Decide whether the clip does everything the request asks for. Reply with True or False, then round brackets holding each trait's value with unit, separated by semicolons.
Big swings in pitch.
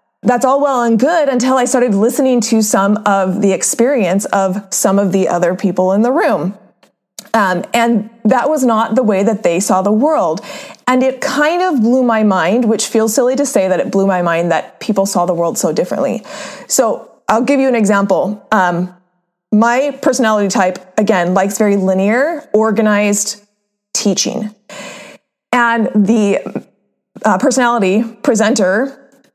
False (4.3 semitones)